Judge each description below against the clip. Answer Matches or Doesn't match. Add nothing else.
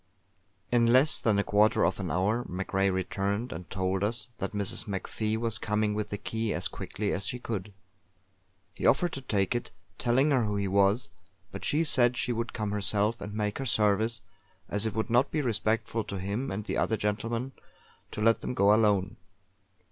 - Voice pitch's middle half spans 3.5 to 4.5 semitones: Doesn't match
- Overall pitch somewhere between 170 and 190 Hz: Doesn't match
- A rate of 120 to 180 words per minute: Doesn't match